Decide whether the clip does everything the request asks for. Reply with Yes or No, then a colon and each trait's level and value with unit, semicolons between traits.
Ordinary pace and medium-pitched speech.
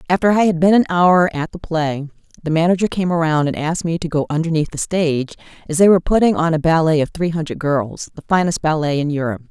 No: fast, 235 wpm; medium, 165 Hz